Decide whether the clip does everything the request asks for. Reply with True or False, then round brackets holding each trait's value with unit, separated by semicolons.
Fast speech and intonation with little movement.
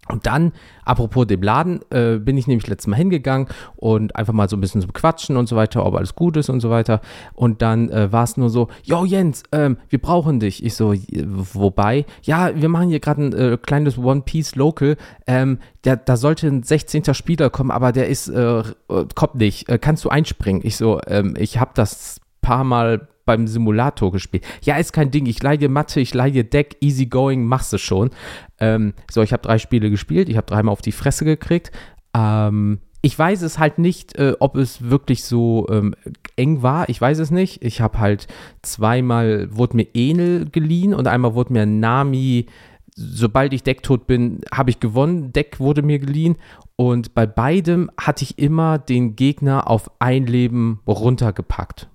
False (195 wpm; 4.7 semitones)